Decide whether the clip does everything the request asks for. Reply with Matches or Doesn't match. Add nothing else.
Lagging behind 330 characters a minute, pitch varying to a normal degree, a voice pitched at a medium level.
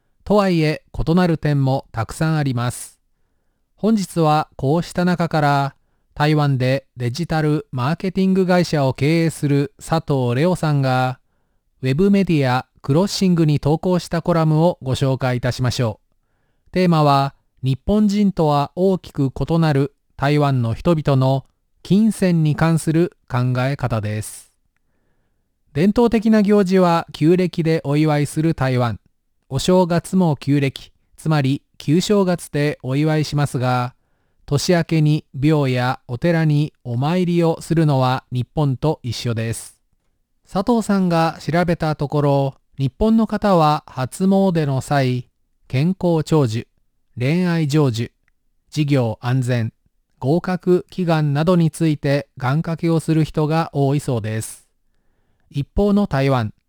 Matches